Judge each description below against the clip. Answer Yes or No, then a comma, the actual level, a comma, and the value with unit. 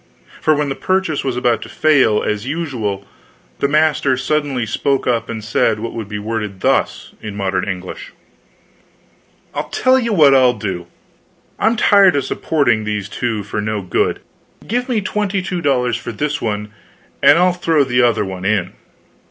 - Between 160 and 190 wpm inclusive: Yes, average, 170 wpm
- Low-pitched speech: Yes, low, 125 Hz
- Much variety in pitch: Yes, wide, 6.6 semitones